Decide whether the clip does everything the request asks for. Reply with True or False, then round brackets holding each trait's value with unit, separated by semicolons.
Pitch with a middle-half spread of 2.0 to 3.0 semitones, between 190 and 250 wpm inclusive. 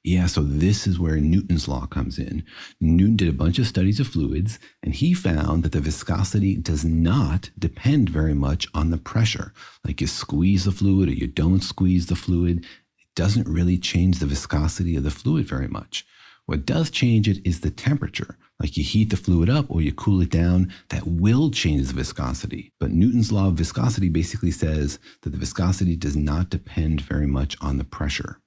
False (4.0 semitones; 200 wpm)